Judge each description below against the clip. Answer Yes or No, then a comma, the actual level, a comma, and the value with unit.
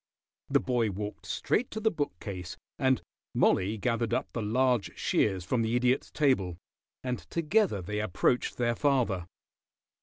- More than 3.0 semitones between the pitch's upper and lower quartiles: Yes, average, 4.6 semitones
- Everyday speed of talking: Yes, average, 145 wpm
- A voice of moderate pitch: No, low, 120 Hz